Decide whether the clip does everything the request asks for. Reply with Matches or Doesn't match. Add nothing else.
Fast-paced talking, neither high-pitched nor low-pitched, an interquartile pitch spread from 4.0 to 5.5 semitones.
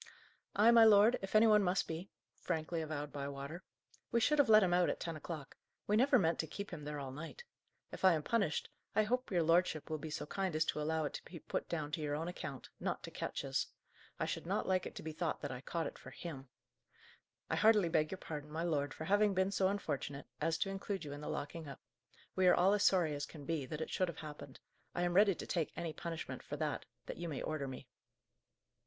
Matches